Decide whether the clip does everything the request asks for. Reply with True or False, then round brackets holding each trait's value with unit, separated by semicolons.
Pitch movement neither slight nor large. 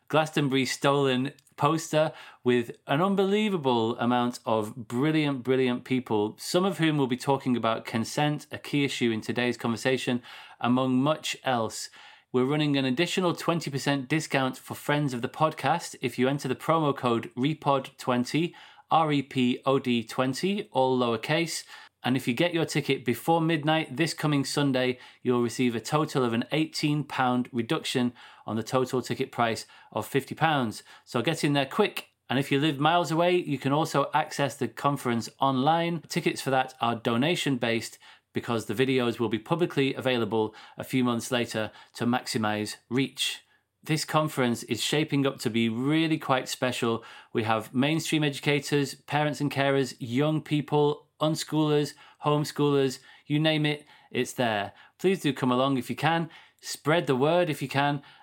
True (3.6 semitones)